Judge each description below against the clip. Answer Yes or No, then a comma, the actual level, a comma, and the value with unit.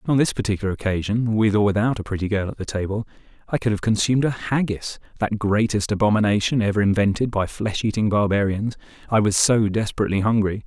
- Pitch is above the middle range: No, low, 105 Hz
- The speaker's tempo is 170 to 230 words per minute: Yes, average, 175 wpm